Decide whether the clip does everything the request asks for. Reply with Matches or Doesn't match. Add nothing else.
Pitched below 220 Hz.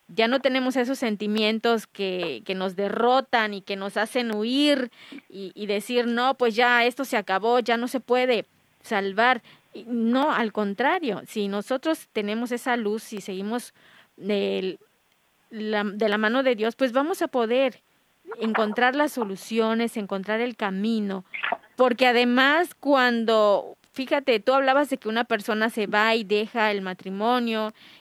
Doesn't match